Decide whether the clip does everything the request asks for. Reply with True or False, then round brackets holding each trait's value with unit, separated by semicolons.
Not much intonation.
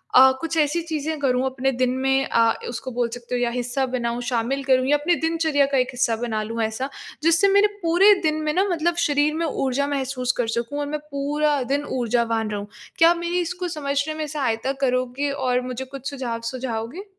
False (3.6 semitones)